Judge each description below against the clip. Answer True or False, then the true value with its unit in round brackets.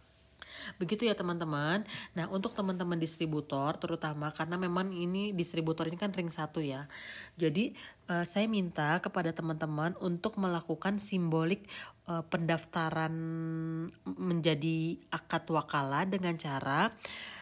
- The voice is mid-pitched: True (170 Hz)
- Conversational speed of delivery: True (115 wpm)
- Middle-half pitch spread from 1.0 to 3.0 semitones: True (2.4 semitones)